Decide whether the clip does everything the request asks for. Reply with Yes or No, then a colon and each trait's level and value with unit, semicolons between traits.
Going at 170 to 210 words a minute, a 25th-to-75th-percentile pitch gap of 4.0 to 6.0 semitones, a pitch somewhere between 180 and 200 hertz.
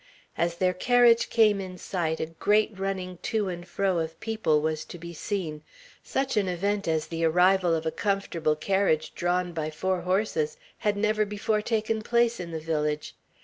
Yes: average, 180 wpm; average, 4.3 semitones; medium, 185 Hz